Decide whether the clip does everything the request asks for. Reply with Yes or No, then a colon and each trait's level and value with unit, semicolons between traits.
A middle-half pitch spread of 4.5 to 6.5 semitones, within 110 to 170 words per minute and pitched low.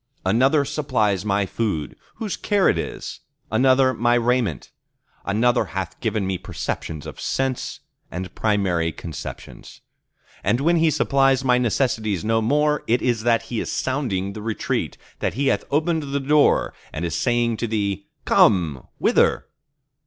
Yes: average, 5.1 semitones; average, 145 wpm; low, 120 Hz